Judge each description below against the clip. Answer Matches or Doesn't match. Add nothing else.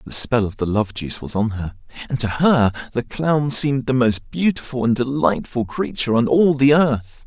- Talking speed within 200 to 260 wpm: Matches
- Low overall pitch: Matches